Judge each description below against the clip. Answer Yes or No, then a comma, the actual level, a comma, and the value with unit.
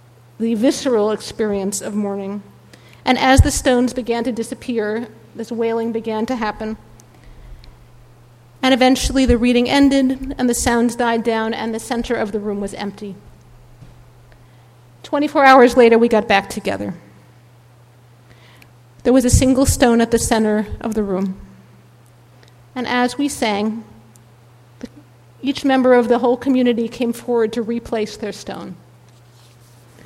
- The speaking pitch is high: Yes, high, 220 Hz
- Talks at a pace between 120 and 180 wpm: Yes, average, 140 wpm